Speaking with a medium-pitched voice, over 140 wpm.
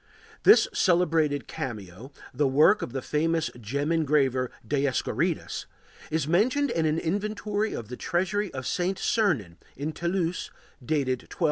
No: medium, 155 Hz; slow, 135 wpm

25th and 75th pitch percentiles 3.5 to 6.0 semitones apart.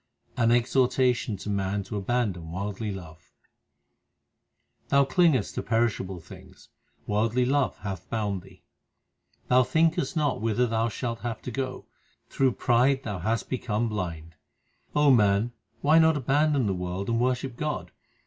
Yes: average, 4.8 semitones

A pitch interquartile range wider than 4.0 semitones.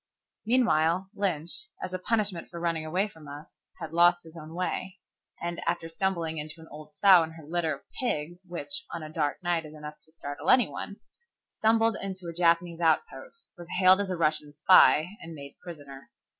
No: average, 3.0 semitones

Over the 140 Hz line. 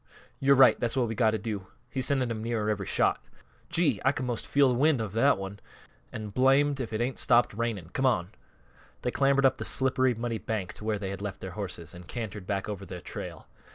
No: low, 115 Hz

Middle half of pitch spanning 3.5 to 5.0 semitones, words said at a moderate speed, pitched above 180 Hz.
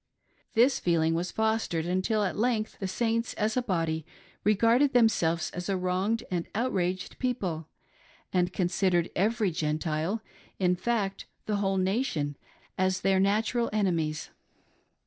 No: average, 4.1 semitones; slow, 130 wpm; high, 190 Hz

